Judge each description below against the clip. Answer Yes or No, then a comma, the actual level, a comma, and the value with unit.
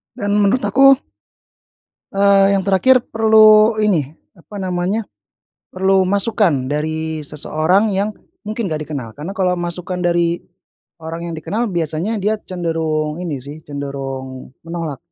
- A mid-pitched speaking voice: Yes, medium, 175 Hz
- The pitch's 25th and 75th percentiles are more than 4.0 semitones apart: Yes, average, 4.5 semitones